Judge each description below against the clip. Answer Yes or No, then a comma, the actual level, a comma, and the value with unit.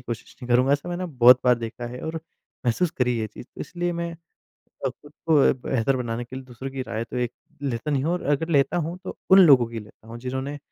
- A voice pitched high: No, low, 130 Hz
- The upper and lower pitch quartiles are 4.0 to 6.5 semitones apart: Yes, average, 4.4 semitones